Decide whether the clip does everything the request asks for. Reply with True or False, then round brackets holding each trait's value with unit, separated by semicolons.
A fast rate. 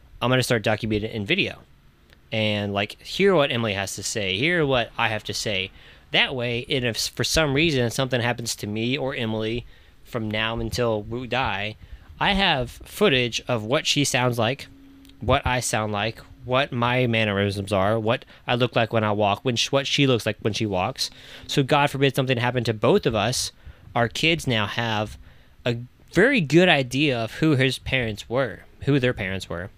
False (195 wpm)